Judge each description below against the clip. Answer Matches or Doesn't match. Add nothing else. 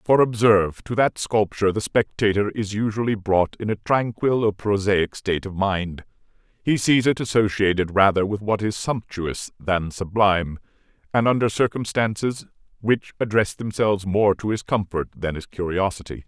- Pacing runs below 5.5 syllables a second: Matches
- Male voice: Matches